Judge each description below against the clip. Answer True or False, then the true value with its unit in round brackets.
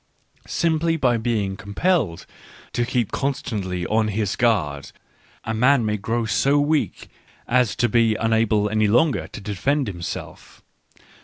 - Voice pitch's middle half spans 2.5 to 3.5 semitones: False (4.1 semitones)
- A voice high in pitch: False (115 Hz)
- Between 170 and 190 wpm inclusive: False (140 wpm)